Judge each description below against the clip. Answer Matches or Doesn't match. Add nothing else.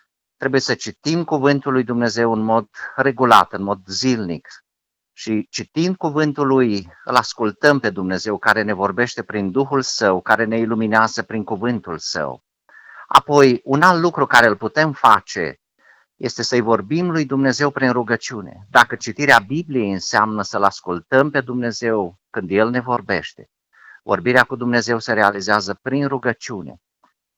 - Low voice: Matches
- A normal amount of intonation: Matches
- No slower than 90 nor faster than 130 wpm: Doesn't match